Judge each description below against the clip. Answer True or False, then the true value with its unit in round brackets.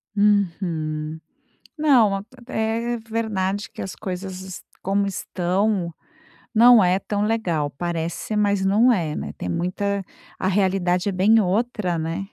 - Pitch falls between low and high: False (195 Hz)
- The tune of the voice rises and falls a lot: False (3.2 semitones)